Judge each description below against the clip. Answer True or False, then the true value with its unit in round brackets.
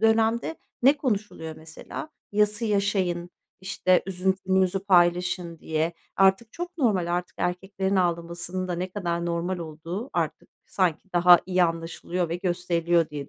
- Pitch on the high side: False (180 Hz)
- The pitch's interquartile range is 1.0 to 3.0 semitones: True (2.6 semitones)